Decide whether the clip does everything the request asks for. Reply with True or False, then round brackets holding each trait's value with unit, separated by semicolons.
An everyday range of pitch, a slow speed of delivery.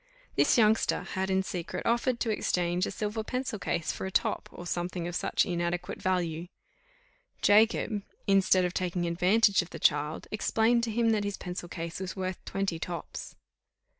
False (3.5 semitones; 170 wpm)